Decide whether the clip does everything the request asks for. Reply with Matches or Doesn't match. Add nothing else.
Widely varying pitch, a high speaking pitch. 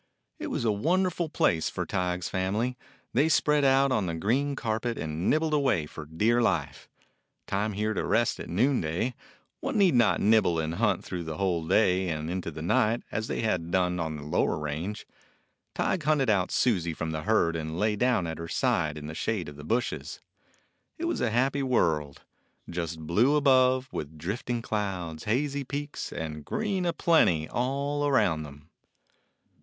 Doesn't match